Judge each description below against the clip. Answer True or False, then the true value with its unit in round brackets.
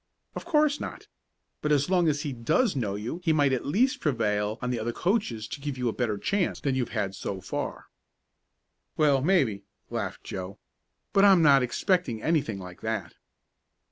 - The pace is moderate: True (180 wpm)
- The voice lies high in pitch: False (135 Hz)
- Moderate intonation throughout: False (7.4 semitones)